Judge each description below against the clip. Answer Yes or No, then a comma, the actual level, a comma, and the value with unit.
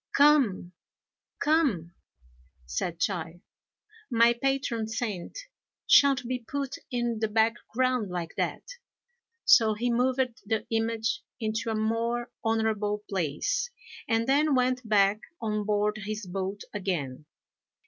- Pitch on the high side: Yes, high, 225 Hz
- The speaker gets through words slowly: Yes, slow, 115 wpm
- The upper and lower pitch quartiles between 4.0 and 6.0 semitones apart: No, average, 3.4 semitones